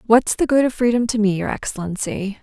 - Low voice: No, high, 225 Hz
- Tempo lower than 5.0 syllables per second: No, 5.8 syllables/s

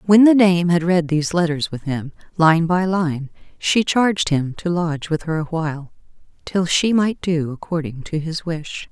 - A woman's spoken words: Yes, female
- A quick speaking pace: No, average, 190 wpm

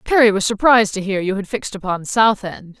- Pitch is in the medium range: No, high, 205 Hz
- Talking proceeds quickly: Yes, fast, 235 wpm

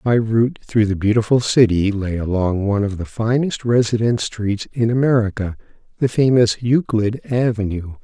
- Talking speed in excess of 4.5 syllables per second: Yes, 5.1 syllables/s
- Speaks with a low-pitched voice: Yes, low, 110 Hz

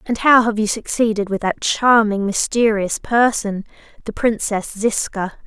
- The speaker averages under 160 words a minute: Yes, average, 145 wpm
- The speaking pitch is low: No, high, 215 Hz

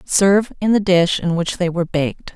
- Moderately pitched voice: Yes, medium, 180 Hz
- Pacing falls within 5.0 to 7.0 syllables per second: Yes, 5.5 syllables/s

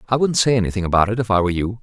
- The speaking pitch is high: No, low, 105 Hz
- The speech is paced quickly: Yes, fast, 330 wpm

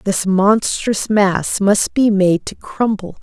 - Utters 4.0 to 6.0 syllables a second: No, 3.2 syllables/s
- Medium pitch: No, high, 200 Hz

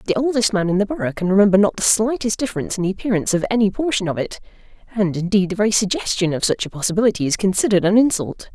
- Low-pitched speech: No, high, 200 Hz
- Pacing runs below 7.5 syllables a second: No, 7.6 syllables/s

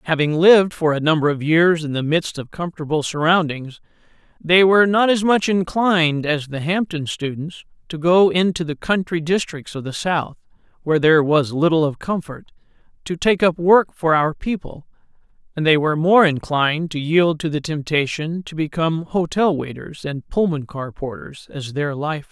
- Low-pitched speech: No, medium, 160 Hz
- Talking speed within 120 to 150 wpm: No, average, 180 wpm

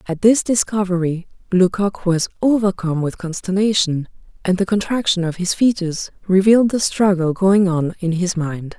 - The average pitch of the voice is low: No, medium, 185 Hz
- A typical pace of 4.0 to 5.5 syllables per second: Yes, 5.1 syllables/s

